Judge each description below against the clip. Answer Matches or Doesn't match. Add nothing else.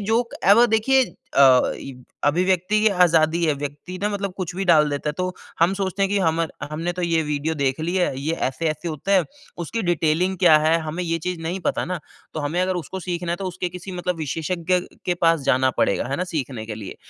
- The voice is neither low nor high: Matches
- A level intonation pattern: Doesn't match